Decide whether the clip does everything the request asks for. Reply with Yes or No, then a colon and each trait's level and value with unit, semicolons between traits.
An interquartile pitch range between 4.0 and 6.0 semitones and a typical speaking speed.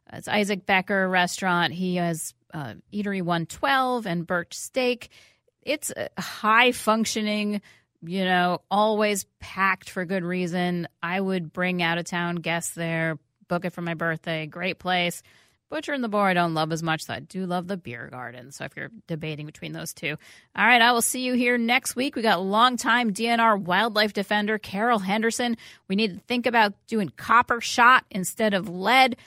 Yes: average, 4.5 semitones; average, 180 wpm